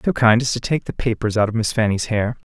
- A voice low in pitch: Yes, low, 115 Hz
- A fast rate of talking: Yes, fast, 310 wpm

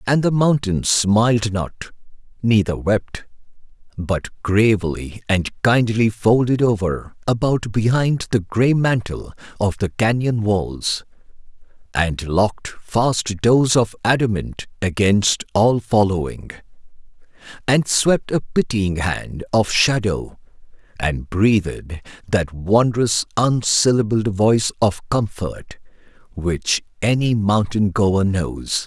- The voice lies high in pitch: No, low, 105 Hz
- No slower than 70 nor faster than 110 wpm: Yes, slow, 105 wpm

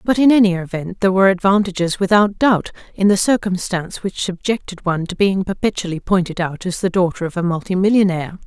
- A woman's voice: Yes, female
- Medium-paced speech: Yes, average, 175 wpm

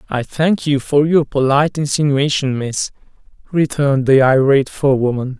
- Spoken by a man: Yes, male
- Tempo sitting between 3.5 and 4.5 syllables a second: No, 5.2 syllables/s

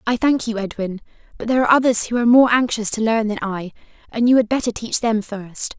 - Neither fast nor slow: No, fast, 240 wpm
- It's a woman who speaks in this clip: Yes, female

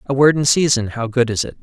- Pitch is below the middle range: Yes, low, 125 Hz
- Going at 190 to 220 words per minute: No, fast, 295 wpm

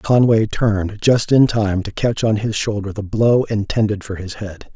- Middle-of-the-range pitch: No, low, 105 Hz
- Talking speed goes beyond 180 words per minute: Yes, average, 200 wpm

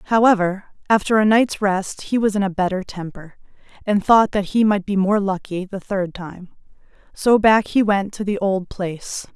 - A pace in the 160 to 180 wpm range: No, average, 190 wpm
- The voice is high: Yes, high, 200 Hz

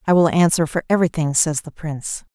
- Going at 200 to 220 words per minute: Yes, fast, 205 wpm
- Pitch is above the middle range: No, medium, 160 Hz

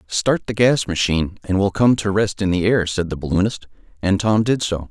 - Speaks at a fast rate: Yes, fast, 230 wpm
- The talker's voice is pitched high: No, low, 100 Hz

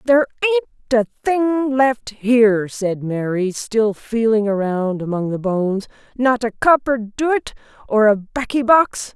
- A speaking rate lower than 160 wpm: Yes, average, 145 wpm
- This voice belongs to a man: No, female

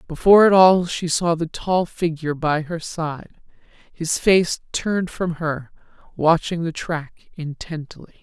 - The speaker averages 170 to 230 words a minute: No, average, 145 wpm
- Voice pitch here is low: No, medium, 165 Hz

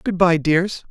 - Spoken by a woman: No, male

